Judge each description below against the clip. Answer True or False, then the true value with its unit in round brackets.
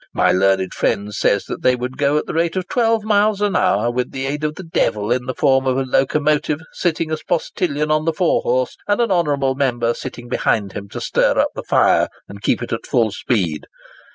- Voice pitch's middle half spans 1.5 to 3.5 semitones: False (5.4 semitones)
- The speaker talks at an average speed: False (225 wpm)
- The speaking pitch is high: False (135 Hz)